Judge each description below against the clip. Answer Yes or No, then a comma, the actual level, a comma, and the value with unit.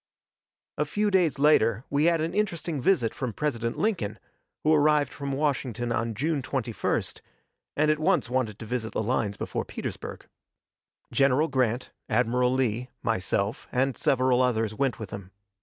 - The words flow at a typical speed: Yes, average, 155 wpm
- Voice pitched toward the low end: Yes, low, 130 Hz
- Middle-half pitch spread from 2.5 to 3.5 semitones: No, average, 4.6 semitones